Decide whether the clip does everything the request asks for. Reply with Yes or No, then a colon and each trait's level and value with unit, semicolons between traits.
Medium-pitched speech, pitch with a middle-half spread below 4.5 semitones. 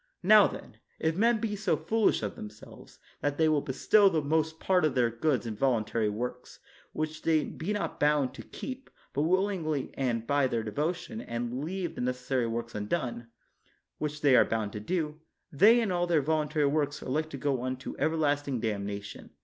No: medium, 145 Hz; average, 4.9 semitones